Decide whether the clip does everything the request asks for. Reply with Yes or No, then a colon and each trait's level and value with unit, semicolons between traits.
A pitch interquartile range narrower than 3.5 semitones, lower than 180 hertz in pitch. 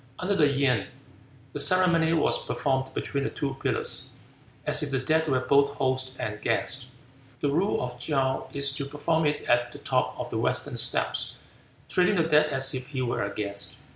Yes: average, 2.7 semitones; medium, 140 Hz